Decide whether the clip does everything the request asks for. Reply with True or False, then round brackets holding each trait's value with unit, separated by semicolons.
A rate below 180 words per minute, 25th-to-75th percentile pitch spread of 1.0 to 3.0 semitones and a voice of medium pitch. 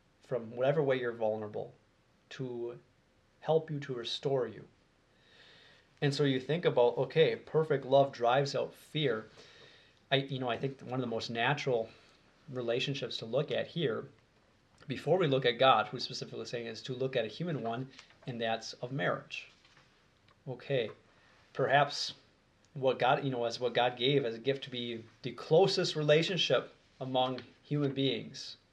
False (165 wpm; 2.7 semitones; 130 Hz)